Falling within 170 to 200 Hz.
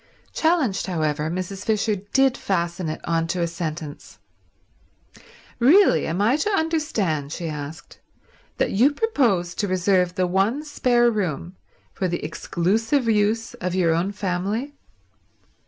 Yes: high, 190 Hz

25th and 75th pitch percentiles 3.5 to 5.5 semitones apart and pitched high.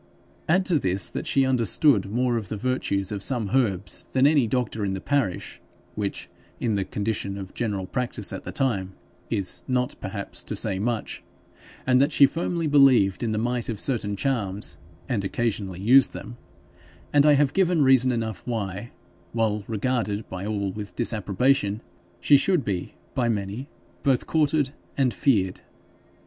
No: average, 4.8 semitones; low, 115 Hz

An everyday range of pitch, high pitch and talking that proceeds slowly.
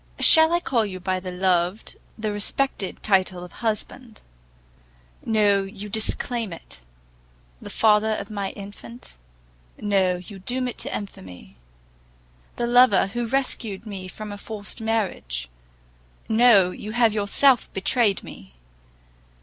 Yes: average, 3.2 semitones; high, 205 Hz; slow, 130 wpm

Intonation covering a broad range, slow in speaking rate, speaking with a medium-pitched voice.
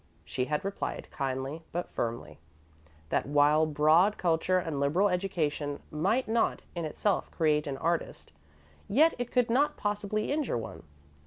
No: wide, 5.9 semitones; average, 145 wpm; medium, 165 Hz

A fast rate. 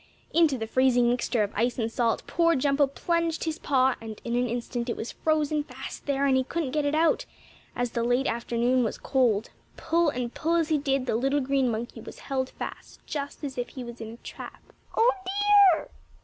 Yes: fast, 210 wpm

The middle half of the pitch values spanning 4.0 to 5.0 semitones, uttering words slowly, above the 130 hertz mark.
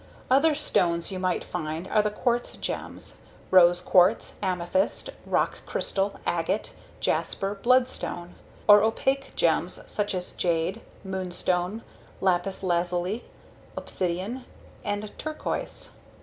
No: average, 3.4 semitones; slow, 105 wpm; high, 190 Hz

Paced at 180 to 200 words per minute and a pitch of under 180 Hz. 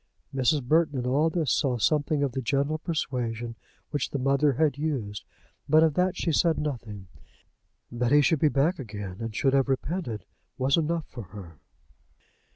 No: average, 170 wpm; low, 135 Hz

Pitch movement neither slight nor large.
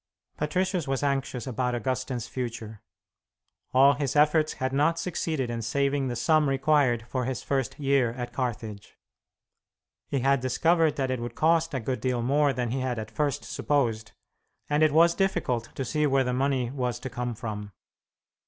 Yes: average, 3.2 semitones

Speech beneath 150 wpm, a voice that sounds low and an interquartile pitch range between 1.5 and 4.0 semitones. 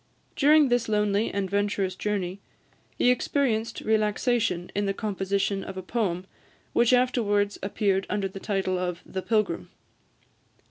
No: slow, 135 wpm; high, 205 Hz; average, 2.7 semitones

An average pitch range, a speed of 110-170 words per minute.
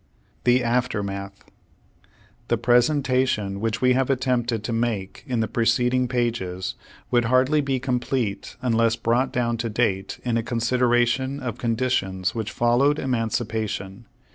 No: narrow, 2.3 semitones; average, 140 wpm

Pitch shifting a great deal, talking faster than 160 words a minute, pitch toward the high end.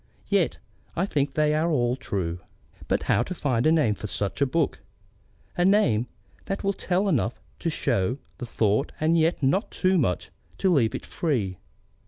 No: wide, 6.9 semitones; average, 180 wpm; medium, 145 Hz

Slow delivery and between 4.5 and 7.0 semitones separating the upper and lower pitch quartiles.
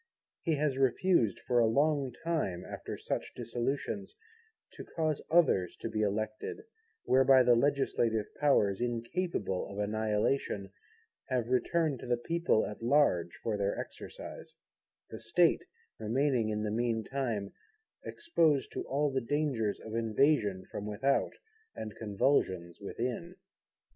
Yes: slow, 130 wpm; average, 5.1 semitones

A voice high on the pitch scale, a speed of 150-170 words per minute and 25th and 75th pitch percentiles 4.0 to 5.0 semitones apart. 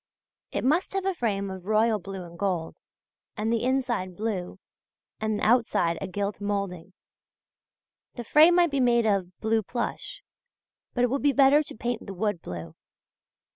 Yes: high, 215 Hz; average, 160 wpm; average, 4.6 semitones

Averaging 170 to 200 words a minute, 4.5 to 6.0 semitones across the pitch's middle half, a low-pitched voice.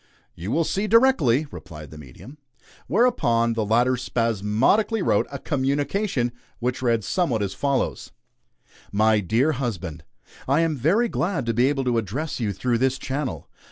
No: average, 155 wpm; average, 5.3 semitones; low, 125 Hz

